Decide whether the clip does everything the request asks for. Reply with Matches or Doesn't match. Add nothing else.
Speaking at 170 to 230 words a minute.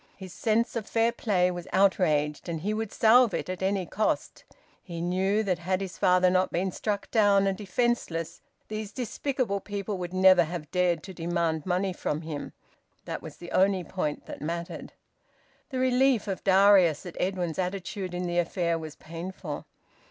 Matches